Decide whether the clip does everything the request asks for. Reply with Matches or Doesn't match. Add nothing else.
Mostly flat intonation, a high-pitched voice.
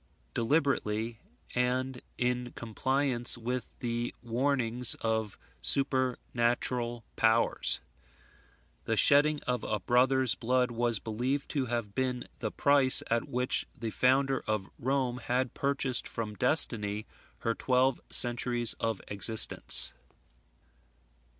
Doesn't match